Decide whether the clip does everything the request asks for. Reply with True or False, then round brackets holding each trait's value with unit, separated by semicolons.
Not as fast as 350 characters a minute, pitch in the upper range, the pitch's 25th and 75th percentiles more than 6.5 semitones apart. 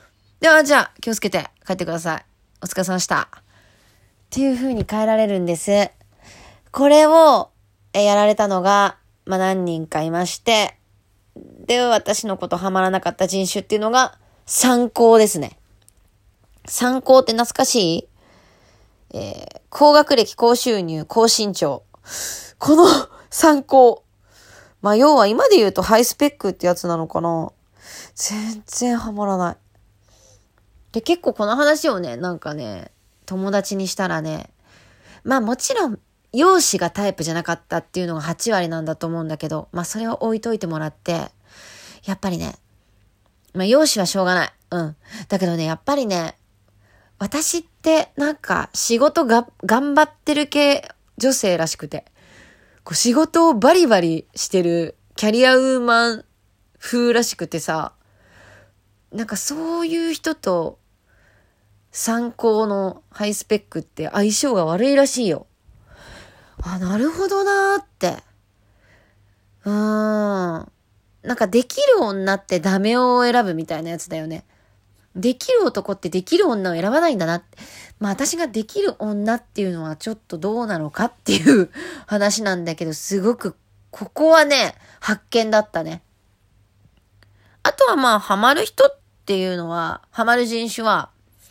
True (275 characters per minute; 195 Hz; 7.2 semitones)